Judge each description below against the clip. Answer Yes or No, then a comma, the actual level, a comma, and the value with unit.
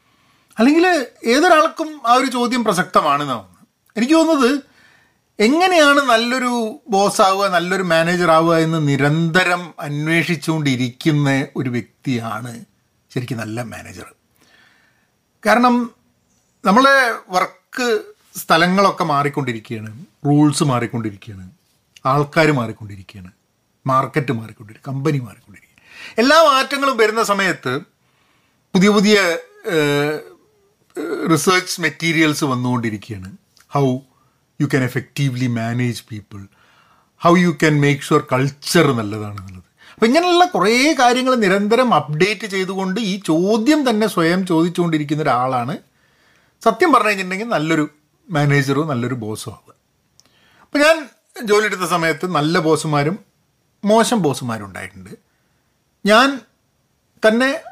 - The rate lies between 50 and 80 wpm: No, average, 95 wpm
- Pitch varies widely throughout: Yes, wide, 9.0 semitones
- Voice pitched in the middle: Yes, medium, 165 Hz